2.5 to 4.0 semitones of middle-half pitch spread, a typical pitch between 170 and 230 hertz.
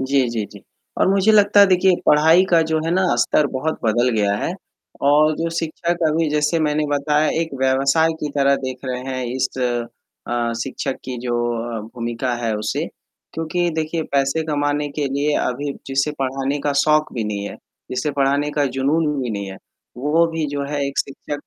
No: average, 3.3 semitones; medium, 145 Hz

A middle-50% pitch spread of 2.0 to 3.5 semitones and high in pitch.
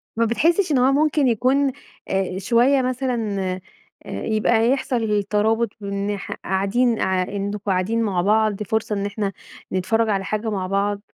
Yes: average, 3.2 semitones; high, 215 Hz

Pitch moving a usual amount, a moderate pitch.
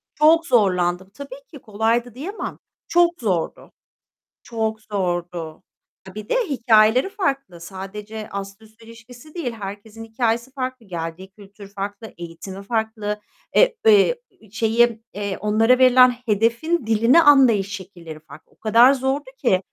No: average, 4.5 semitones; high, 220 Hz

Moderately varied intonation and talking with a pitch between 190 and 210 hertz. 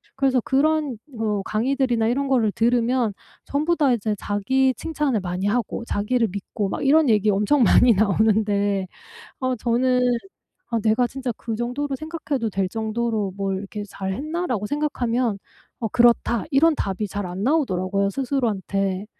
No: average, 4.6 semitones; high, 230 Hz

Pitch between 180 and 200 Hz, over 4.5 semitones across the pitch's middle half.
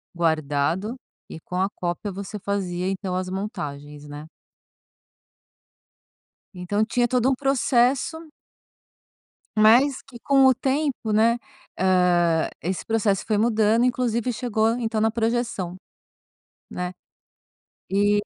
No: high, 210 Hz; average, 4.9 semitones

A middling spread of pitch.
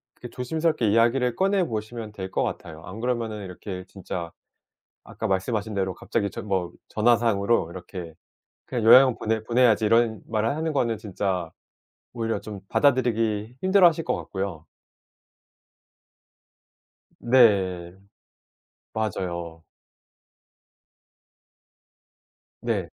Yes: average, 4.1 semitones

